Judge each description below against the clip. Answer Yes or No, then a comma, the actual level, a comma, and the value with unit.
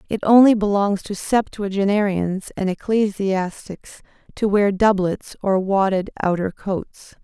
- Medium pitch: No, high, 195 Hz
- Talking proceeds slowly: Yes, slow, 115 wpm